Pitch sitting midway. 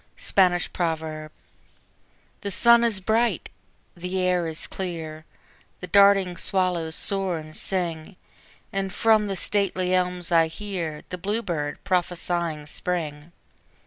Yes: medium, 180 Hz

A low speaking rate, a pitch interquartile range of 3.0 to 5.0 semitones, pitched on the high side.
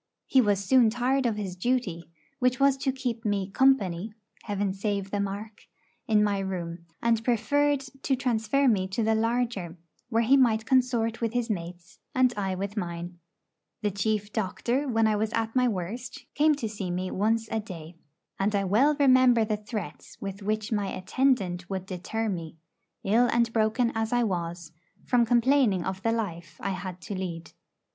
No: average, 180 wpm; average, 4.1 semitones; high, 215 Hz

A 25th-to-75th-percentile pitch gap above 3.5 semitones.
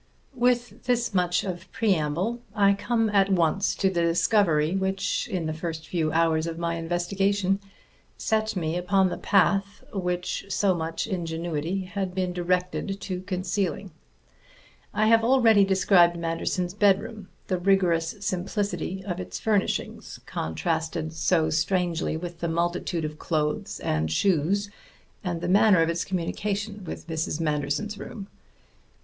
No: average, 3.2 semitones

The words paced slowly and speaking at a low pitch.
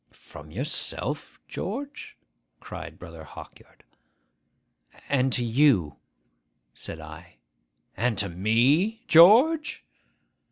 Yes: slow, 85 wpm; low, 125 Hz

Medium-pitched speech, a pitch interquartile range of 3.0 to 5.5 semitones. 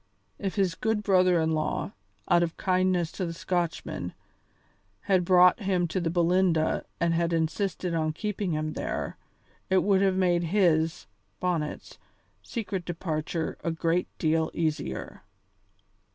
No: medium, 175 Hz; narrow, 2.4 semitones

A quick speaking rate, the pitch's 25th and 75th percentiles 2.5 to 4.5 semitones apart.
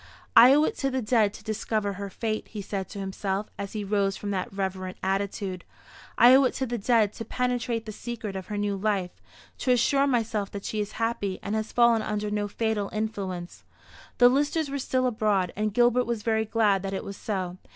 Yes: fast, 215 wpm; average, 3.0 semitones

